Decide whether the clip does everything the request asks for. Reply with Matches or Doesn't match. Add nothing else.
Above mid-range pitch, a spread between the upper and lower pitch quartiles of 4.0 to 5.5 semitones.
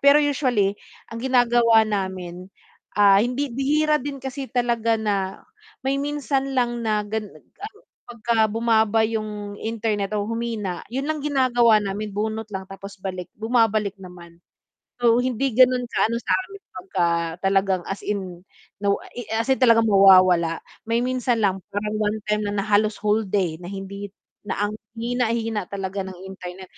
Doesn't match